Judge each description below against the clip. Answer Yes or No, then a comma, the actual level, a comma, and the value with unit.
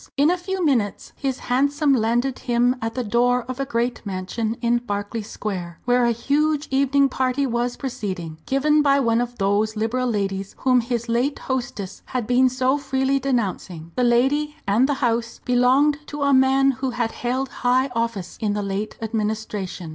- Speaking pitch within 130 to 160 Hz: No, high, 245 Hz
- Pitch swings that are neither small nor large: Yes, average, 3.4 semitones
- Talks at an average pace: Yes, average, 175 wpm